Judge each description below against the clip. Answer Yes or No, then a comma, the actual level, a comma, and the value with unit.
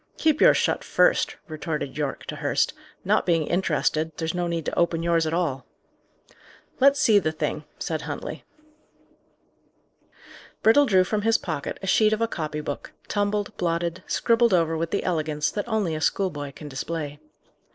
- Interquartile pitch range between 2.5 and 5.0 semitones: Yes, average, 4.7 semitones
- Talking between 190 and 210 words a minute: No, average, 165 wpm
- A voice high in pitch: No, medium, 170 Hz